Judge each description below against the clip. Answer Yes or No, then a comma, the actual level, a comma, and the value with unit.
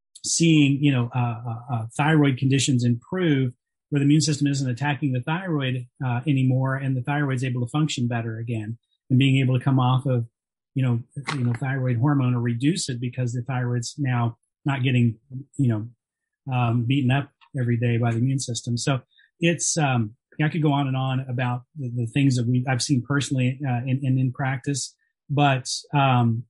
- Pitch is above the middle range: No, low, 130 Hz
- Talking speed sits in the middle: Yes, average, 190 wpm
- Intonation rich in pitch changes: No, narrow, 2.5 semitones